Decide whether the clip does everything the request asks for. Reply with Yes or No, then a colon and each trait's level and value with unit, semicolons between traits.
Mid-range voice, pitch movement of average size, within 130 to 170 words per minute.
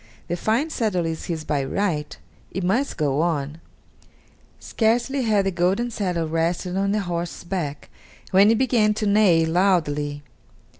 Yes: medium, 180 Hz; average, 4.5 semitones; average, 150 wpm